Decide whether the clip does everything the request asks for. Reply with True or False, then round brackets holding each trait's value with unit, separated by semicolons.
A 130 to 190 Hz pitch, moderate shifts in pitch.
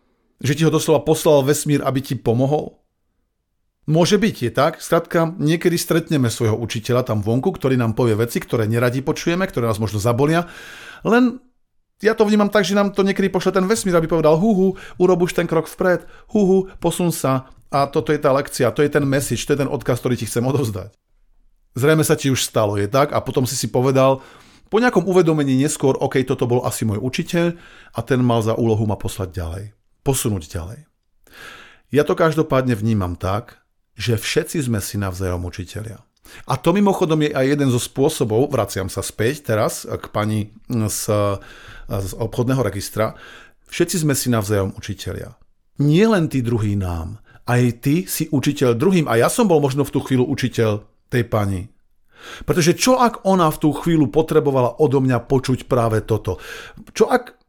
False (135 Hz; 6.4 semitones)